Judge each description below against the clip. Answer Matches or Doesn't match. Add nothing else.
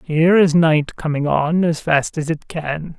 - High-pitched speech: Doesn't match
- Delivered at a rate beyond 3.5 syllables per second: Matches